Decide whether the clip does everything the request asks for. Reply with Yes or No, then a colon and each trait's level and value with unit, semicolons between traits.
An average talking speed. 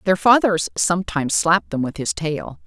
Yes: average, 180 wpm